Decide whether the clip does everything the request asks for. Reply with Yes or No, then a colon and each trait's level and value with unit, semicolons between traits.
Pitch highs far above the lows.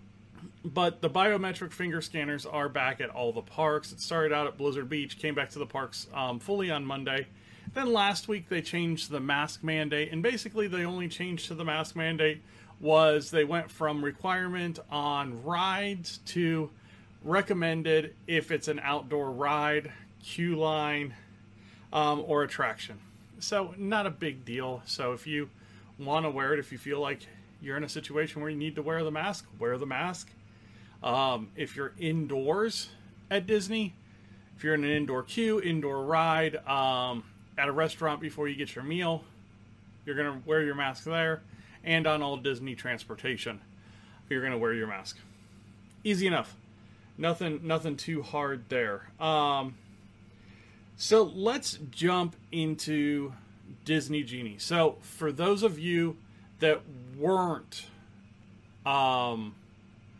Yes: wide, 6.3 semitones